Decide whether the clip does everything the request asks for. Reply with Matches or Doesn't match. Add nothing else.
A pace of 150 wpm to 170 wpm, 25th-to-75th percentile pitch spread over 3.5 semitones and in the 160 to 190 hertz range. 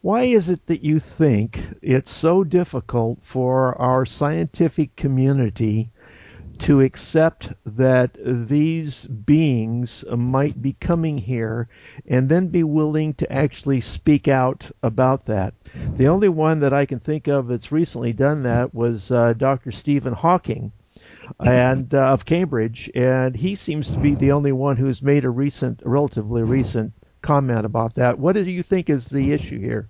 Doesn't match